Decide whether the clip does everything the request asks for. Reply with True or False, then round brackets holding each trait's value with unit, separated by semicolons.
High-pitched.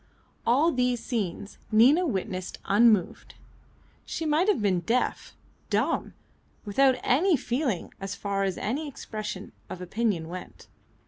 True (220 Hz)